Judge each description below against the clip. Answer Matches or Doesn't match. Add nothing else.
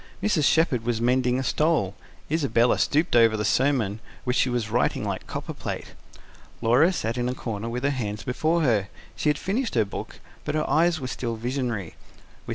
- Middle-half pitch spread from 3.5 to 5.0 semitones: Matches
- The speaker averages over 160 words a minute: Matches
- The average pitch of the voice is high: Doesn't match